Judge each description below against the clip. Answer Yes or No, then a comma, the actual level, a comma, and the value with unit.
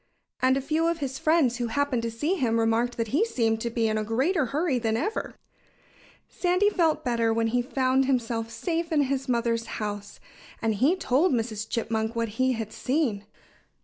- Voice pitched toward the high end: Yes, high, 245 Hz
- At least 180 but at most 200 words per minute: Yes, average, 190 wpm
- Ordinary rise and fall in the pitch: Yes, average, 4.3 semitones